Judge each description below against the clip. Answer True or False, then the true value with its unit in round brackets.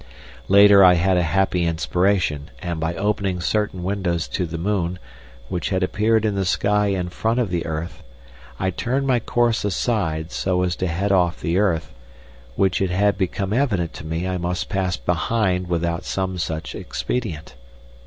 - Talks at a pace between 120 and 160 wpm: False (175 wpm)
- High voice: False (95 Hz)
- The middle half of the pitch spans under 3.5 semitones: True (3.0 semitones)